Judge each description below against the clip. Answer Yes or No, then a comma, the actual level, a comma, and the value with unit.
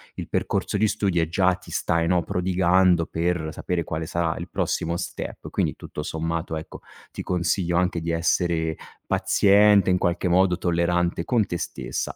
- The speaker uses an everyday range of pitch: No, narrow, 1.7 semitones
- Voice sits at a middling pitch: No, very low, 85 Hz